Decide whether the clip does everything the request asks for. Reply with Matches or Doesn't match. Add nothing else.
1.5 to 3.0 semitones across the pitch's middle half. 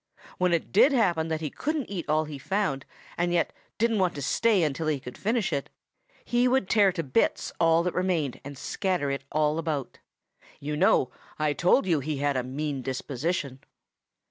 Doesn't match